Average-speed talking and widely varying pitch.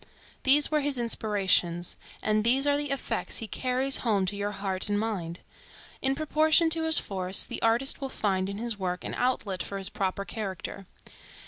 Yes: average, 185 wpm; wide, 5.8 semitones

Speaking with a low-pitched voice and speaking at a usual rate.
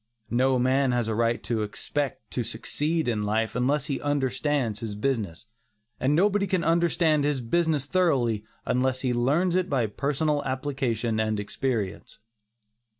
Yes: low, 130 Hz; average, 150 wpm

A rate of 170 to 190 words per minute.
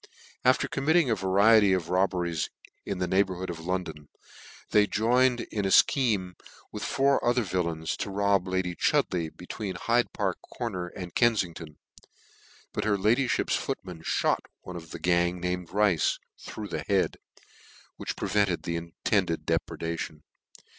No: average, 150 wpm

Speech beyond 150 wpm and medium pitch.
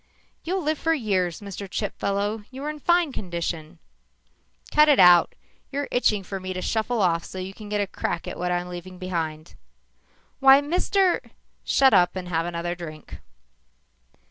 No: average, 170 wpm; high, 195 Hz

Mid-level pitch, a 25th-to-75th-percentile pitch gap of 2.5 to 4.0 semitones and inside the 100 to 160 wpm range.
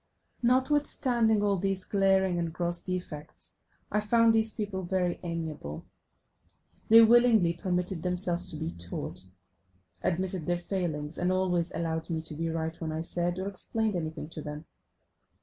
Yes: medium, 180 Hz; average, 3.4 semitones; average, 150 wpm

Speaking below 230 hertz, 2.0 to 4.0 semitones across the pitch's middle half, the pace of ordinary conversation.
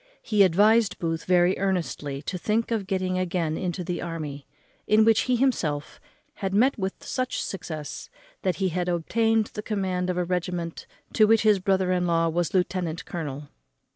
Yes: medium, 185 Hz; average, 3.6 semitones; average, 170 wpm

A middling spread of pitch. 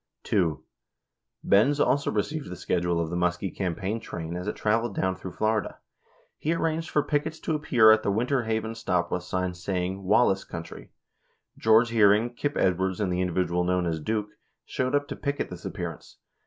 Yes: average, 4.5 semitones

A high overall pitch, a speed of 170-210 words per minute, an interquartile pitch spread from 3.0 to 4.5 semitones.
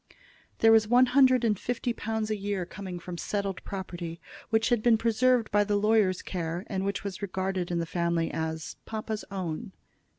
Yes: high, 200 Hz; average, 185 wpm; average, 3.7 semitones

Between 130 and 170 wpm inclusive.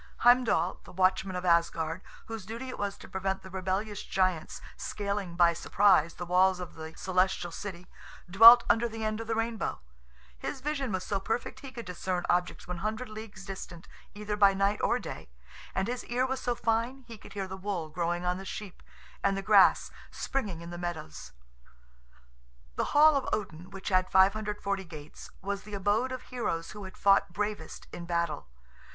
No: average, 180 wpm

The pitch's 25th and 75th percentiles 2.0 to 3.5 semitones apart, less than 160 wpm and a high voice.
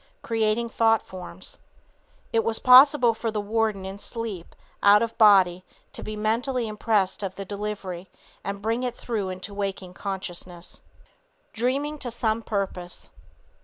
Yes: average, 3.1 semitones; average, 145 wpm; high, 210 Hz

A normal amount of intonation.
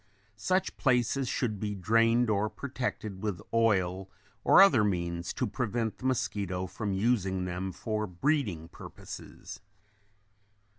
Yes: average, 4.3 semitones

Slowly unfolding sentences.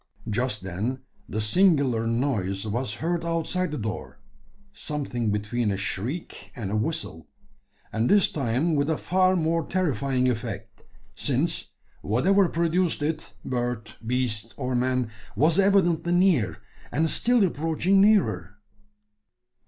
Yes: slow, 125 wpm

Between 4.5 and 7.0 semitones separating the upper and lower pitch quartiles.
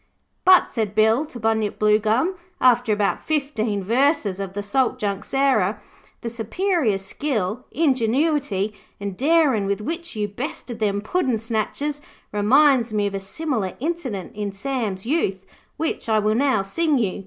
Yes: wide, 5.6 semitones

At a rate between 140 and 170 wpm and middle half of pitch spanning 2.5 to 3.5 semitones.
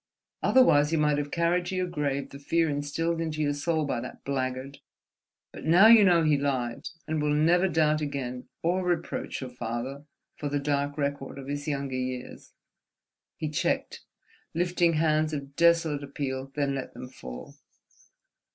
Yes: average, 160 wpm; average, 2.9 semitones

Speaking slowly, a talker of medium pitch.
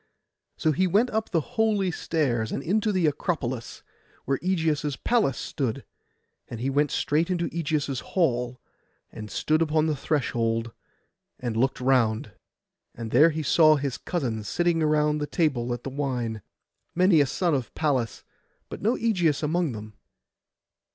No: average, 150 wpm; medium, 150 Hz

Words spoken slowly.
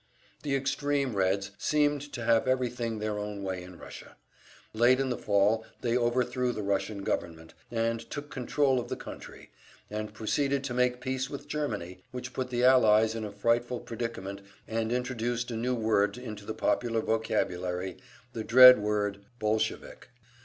No: average, 160 wpm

